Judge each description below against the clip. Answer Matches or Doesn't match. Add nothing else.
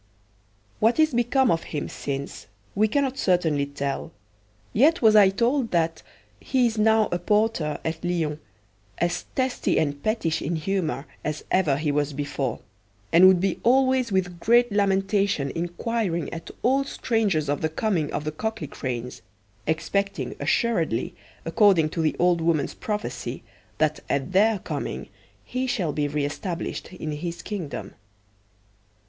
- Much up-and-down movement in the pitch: Matches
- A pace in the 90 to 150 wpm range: Matches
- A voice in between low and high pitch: Matches